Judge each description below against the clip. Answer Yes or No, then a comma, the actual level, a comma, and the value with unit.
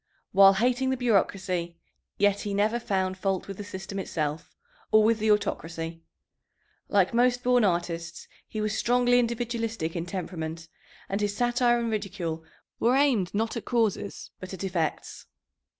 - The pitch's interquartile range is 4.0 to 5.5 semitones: Yes, average, 4.4 semitones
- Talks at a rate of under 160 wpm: Yes, average, 150 wpm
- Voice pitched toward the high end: Yes, high, 205 Hz